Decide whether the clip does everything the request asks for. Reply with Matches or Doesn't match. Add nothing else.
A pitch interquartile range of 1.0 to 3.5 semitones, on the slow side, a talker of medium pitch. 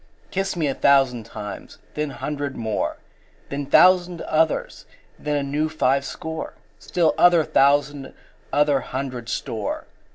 Matches